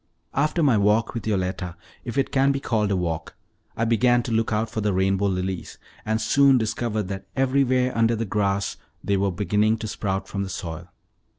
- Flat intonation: No, average, 3.7 semitones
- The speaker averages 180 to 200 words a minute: Yes, average, 195 wpm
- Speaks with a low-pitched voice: Yes, low, 105 Hz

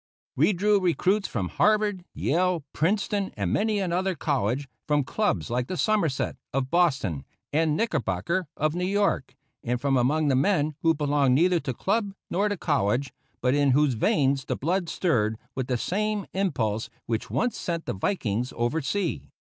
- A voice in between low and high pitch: Yes, medium, 155 Hz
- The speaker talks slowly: No, average, 165 wpm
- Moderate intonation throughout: No, wide, 6.7 semitones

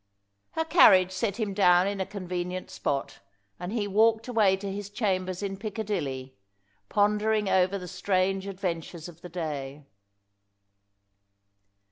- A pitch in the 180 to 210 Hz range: Yes, high, 190 Hz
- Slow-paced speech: Yes, slow, 130 wpm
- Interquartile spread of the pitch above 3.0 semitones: No, narrow, 2.5 semitones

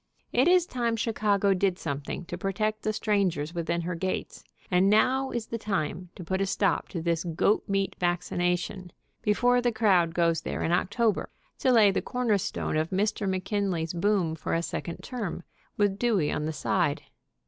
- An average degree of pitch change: Yes, average, 3.9 semitones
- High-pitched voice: Yes, high, 195 Hz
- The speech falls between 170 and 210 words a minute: Yes, average, 175 wpm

